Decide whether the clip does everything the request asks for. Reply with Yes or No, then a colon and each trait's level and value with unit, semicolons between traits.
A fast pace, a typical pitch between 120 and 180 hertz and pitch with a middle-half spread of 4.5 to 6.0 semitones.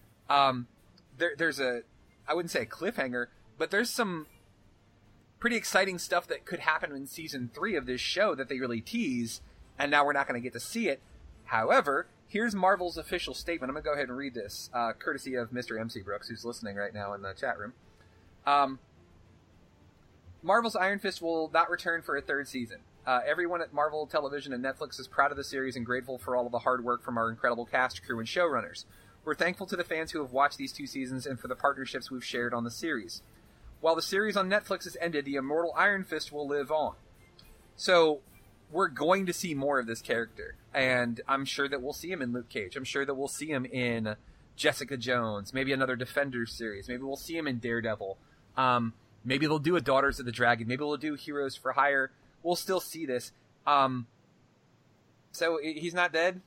Yes: fast, 210 wpm; low, 135 Hz; average, 4.9 semitones